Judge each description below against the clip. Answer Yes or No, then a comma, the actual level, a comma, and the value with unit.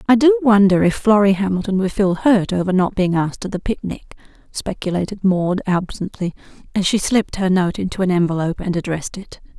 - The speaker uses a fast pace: No, average, 190 wpm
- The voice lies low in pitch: No, high, 195 Hz